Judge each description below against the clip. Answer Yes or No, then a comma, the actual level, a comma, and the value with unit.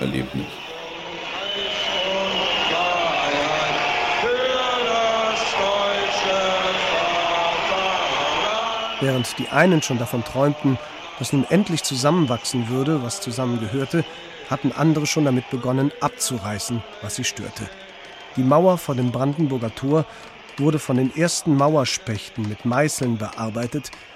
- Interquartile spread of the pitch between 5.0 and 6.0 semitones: Yes, wide, 5.4 semitones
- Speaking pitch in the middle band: Yes, medium, 145 Hz